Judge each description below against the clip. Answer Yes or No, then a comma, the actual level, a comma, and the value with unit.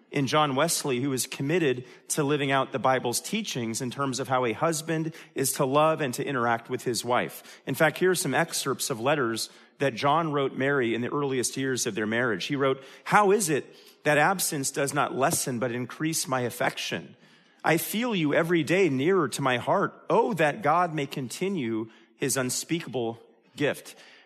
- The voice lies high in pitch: No, medium, 140 Hz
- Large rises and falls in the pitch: No, average, 3.8 semitones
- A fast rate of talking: No, average, 190 wpm